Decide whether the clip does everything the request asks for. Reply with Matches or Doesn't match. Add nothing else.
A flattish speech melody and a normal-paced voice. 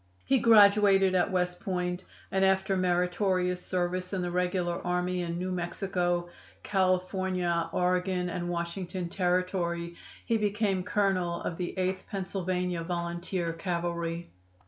Doesn't match